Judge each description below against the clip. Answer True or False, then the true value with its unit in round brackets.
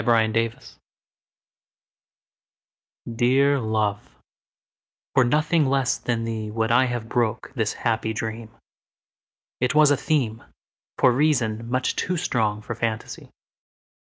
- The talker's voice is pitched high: False (115 Hz)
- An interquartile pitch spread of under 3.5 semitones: True (2.8 semitones)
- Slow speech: True (105 wpm)